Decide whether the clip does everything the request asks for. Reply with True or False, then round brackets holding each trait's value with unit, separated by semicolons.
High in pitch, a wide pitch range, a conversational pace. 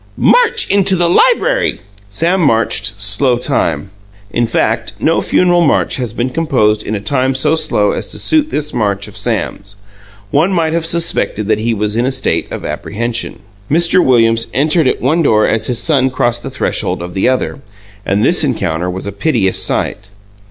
False (120 Hz; 7.3 semitones; 180 wpm)